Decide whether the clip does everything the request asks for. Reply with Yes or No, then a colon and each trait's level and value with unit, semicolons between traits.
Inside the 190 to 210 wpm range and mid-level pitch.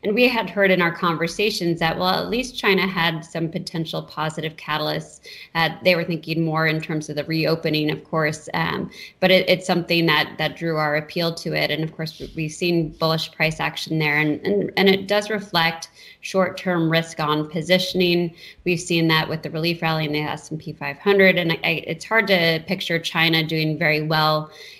Yes: average, 200 wpm; medium, 165 Hz